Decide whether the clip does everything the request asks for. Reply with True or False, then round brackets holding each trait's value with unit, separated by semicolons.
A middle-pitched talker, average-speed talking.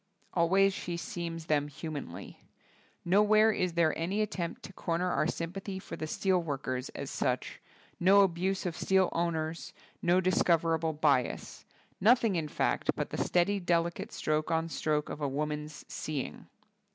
True (170 Hz; 160 wpm)